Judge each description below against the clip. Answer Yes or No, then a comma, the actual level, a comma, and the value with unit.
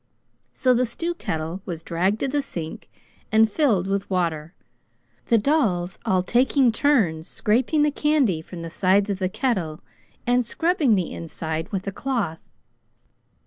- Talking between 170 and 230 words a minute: No, average, 150 wpm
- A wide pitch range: Yes, wide, 6.9 semitones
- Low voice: No, high, 200 Hz